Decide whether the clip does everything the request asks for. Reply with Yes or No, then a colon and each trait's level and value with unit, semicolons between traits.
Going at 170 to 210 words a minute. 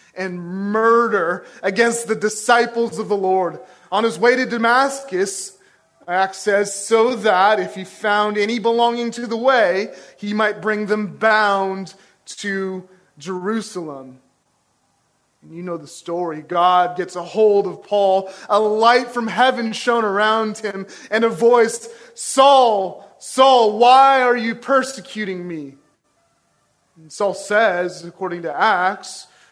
No: slow, 135 wpm